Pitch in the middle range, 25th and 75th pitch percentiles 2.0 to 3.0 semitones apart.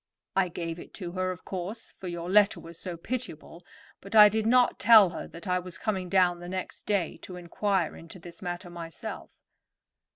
Yes: medium, 180 Hz; narrow, 2.6 semitones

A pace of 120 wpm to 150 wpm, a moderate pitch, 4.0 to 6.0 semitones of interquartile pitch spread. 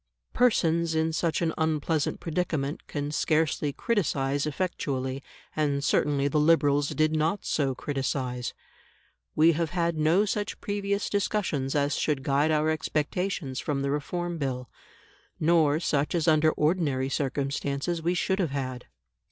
No: slow, 135 wpm; medium, 155 Hz; average, 3.1 semitones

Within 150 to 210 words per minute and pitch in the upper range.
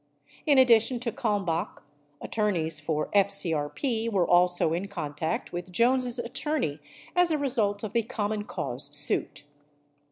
No: slow, 135 wpm; high, 205 Hz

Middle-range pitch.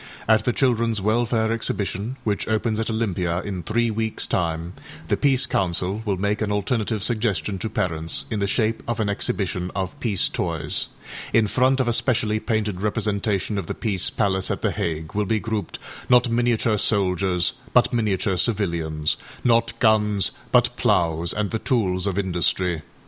No: low, 105 Hz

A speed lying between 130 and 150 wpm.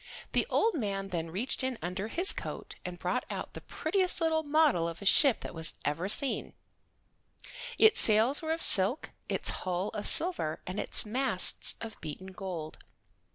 No: average, 170 wpm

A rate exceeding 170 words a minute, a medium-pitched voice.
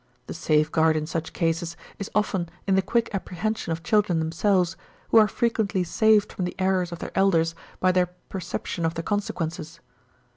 Yes: average, 180 wpm; medium, 180 Hz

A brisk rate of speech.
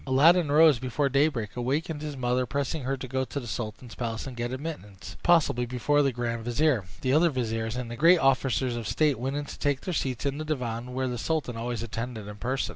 Yes: fast, 235 wpm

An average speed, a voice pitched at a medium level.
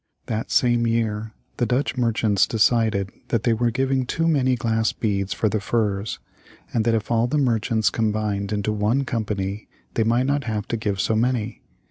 No: average, 180 wpm; low, 115 Hz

